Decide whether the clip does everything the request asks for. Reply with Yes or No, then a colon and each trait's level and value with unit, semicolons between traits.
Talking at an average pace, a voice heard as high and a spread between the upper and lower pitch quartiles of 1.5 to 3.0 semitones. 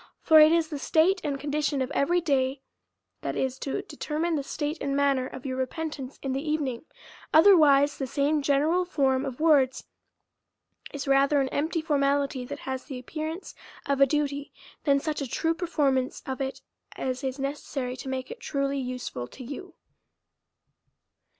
Yes: average, 175 wpm; very high, 280 Hz; narrow, 2.6 semitones